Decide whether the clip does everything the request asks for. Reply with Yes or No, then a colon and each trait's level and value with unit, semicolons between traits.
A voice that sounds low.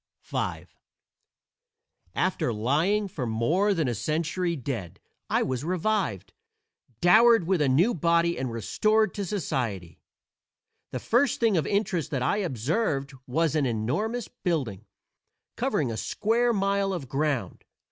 No: medium, 165 Hz